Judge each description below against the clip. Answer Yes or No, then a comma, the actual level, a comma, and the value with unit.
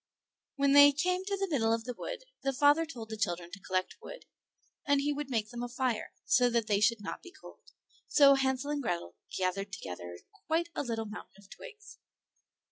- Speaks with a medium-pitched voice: No, very high, 250 Hz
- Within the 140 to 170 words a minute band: No, fast, 205 wpm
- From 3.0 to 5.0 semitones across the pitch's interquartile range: No, wide, 5.6 semitones